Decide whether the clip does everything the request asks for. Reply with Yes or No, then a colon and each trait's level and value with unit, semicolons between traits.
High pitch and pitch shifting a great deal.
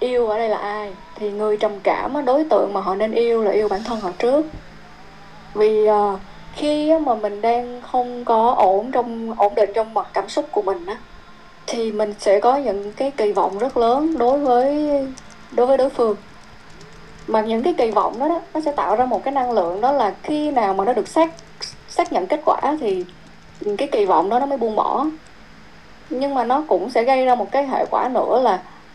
No: high, 240 Hz; average, 4.7 semitones